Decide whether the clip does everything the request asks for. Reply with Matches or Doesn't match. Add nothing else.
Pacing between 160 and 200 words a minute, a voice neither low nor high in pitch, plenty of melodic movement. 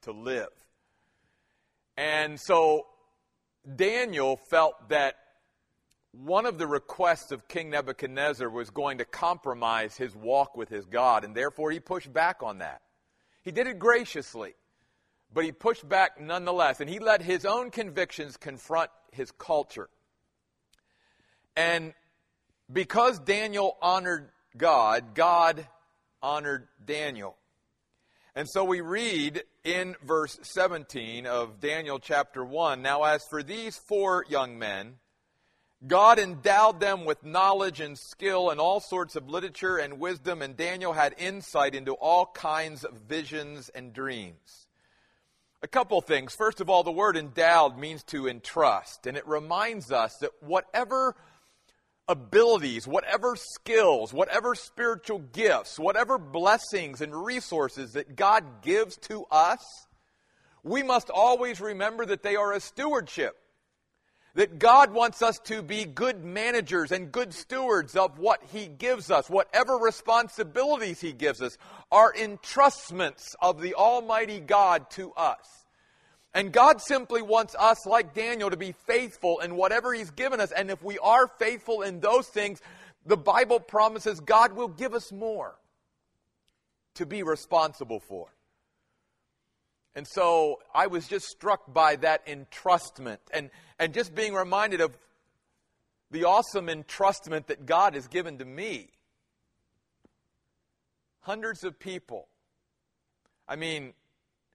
Doesn't match